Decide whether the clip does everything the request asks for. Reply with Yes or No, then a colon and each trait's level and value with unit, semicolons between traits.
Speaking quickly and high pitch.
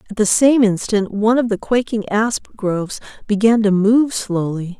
No: average, 175 wpm; high, 215 Hz